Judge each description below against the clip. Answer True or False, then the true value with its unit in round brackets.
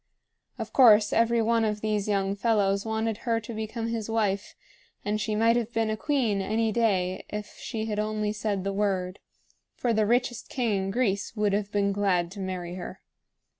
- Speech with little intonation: True (2.2 semitones)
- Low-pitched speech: False (210 Hz)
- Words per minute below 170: False (190 wpm)